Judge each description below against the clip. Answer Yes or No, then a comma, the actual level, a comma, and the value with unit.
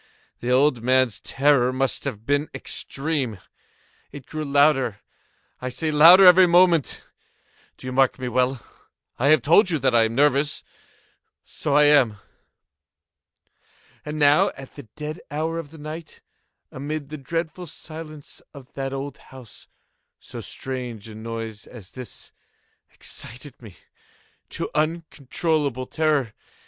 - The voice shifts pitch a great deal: No, average, 3.4 semitones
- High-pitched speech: No, medium, 140 Hz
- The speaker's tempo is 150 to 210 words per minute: No, slow, 135 wpm